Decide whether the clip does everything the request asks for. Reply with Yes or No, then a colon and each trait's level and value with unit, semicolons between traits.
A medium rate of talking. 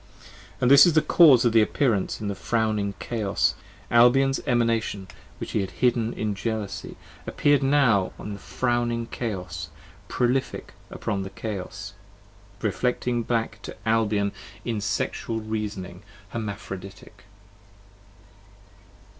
No: slow, 120 wpm